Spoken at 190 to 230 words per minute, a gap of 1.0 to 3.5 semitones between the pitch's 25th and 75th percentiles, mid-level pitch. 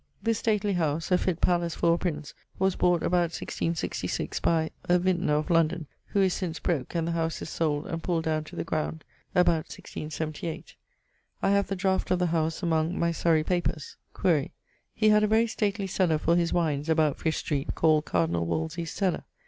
Yes: average, 195 wpm; narrow, 2.4 semitones; medium, 170 Hz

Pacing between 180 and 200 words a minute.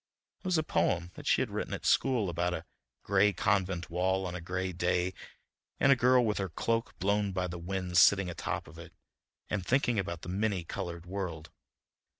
Yes: average, 195 wpm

